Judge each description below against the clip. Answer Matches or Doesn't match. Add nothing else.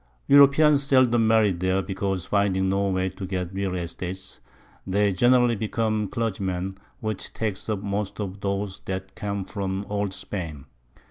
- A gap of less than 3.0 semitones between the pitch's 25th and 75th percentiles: Matches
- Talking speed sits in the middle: Matches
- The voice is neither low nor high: Doesn't match